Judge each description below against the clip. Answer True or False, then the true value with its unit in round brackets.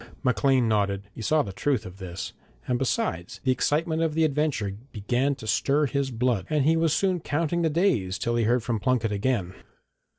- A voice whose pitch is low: True (130 Hz)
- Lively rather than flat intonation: True (6.2 semitones)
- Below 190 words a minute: False (195 wpm)